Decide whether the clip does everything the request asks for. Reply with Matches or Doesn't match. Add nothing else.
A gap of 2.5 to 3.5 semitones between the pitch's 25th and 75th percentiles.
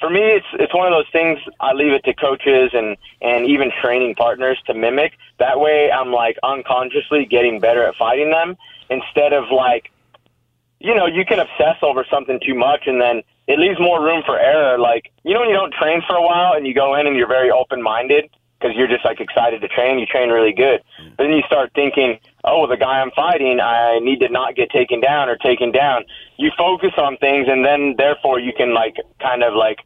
Doesn't match